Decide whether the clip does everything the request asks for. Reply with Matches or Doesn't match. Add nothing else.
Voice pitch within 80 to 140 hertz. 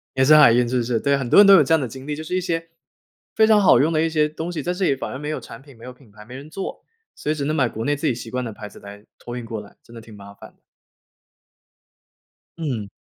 Matches